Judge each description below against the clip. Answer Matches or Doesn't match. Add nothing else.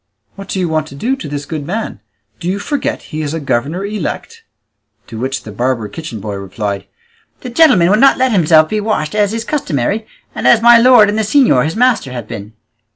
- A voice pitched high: Doesn't match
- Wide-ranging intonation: Matches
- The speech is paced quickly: Matches